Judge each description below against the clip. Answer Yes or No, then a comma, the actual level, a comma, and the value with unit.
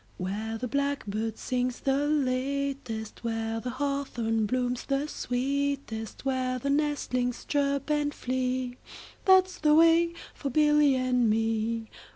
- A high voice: Yes, very high, 255 Hz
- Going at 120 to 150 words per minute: Yes, slow, 135 wpm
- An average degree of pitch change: Yes, average, 3.5 semitones